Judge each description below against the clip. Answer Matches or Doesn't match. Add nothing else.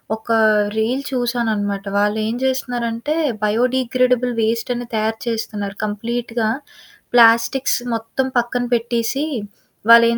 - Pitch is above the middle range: Matches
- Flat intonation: Matches